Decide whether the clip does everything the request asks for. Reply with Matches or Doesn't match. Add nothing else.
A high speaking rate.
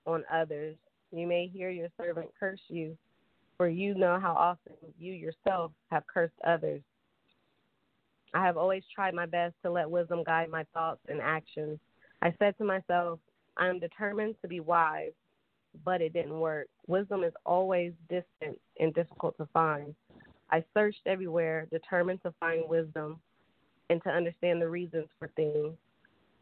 Doesn't match